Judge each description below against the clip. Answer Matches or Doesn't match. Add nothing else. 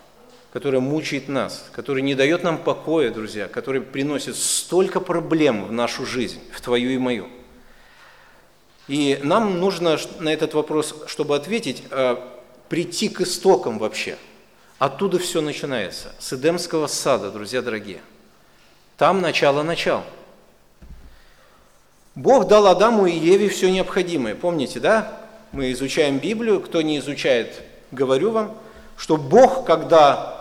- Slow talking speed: Doesn't match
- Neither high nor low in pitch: Matches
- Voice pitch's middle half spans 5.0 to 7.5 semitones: Matches